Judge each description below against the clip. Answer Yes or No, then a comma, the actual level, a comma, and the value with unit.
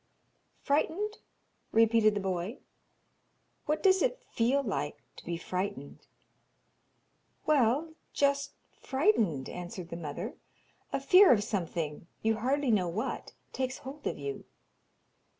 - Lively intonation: Yes, wide, 8.1 semitones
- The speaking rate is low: Yes, slow, 115 wpm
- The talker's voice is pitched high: Yes, high, 225 Hz